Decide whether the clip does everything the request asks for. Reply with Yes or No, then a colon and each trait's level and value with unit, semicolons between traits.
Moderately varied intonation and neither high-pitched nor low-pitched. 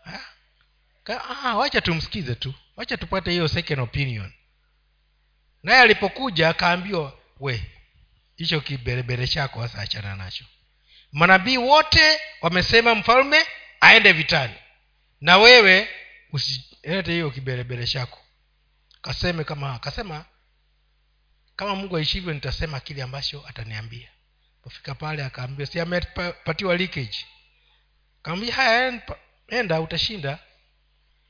No: wide, 7.0 semitones; medium, 145 Hz